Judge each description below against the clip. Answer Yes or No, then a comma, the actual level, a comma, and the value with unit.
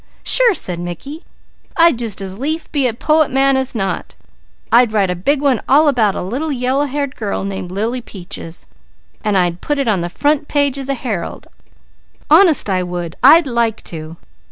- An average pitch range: No, wide, 6.9 semitones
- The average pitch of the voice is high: Yes, high, 245 Hz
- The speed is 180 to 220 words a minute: Yes, average, 185 wpm